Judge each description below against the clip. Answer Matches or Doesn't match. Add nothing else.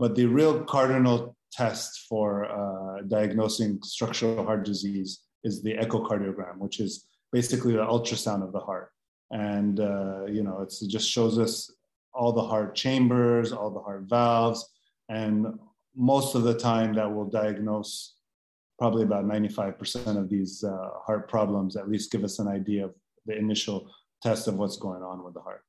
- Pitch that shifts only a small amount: Matches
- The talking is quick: Doesn't match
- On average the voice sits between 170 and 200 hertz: Doesn't match